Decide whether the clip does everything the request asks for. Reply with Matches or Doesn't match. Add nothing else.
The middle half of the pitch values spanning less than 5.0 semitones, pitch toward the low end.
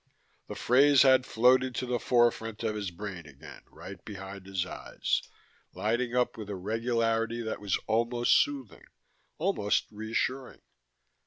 Matches